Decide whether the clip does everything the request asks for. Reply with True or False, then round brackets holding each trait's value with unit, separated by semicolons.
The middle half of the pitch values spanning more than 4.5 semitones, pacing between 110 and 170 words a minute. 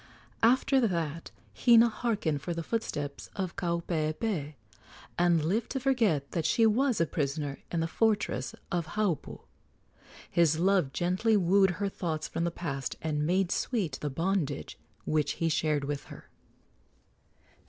True (5.2 semitones; 145 wpm)